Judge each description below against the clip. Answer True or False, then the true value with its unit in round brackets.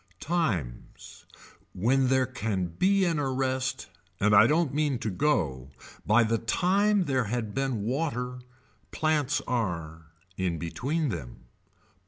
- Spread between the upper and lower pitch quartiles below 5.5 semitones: False (6.5 semitones)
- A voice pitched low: True (125 Hz)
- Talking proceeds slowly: True (125 wpm)